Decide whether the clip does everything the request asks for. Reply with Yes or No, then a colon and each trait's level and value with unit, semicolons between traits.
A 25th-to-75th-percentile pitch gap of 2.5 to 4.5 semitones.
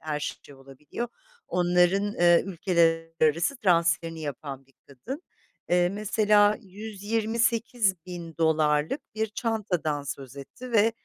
No: wide, 5.4 semitones